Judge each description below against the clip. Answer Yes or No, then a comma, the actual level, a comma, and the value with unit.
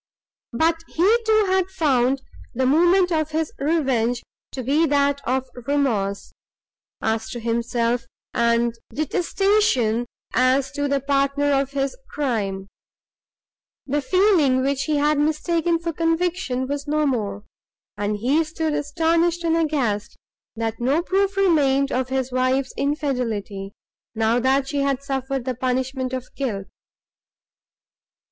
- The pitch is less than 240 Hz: No, very high, 275 Hz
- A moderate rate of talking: No, slow, 130 wpm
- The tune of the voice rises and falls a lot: No, average, 4.1 semitones